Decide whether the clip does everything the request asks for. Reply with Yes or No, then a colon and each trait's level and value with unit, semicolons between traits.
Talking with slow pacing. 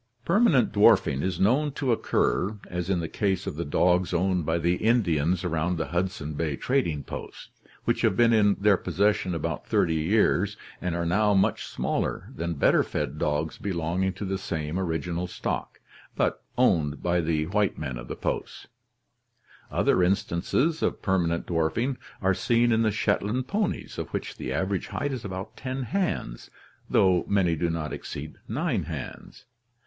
No: average, 165 wpm